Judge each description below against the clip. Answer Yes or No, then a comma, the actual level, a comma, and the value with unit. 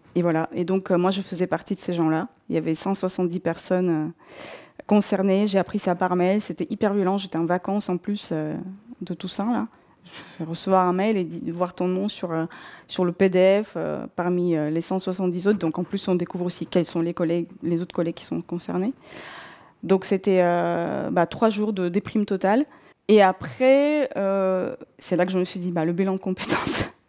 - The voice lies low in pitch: No, medium, 185 Hz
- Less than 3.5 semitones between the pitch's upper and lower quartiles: Yes, narrow, 2.5 semitones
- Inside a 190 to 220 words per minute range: Yes, average, 215 wpm